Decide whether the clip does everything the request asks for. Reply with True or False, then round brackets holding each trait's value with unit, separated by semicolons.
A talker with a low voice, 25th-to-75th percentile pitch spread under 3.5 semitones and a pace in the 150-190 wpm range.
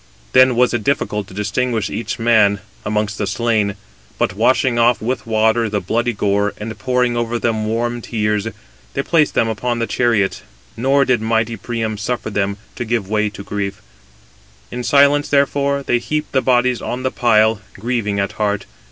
True (115 Hz; 2.7 semitones; 175 wpm)